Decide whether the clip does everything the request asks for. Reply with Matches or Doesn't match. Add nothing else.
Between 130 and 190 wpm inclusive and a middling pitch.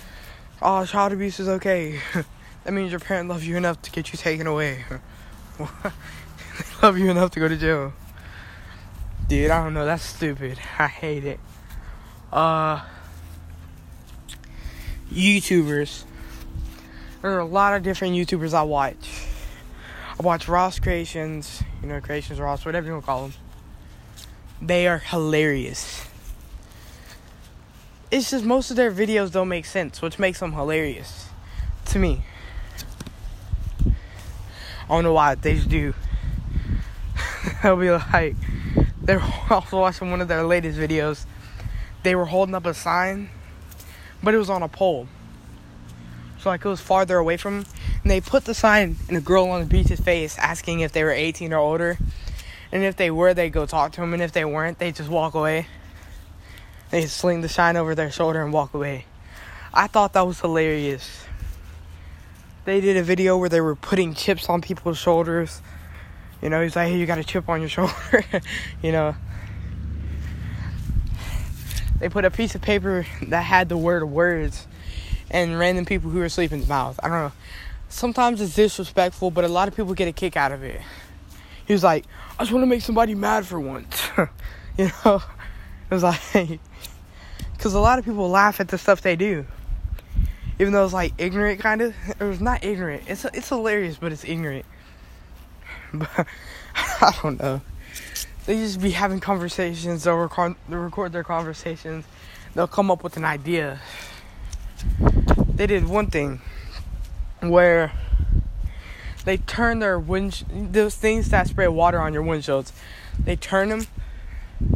Matches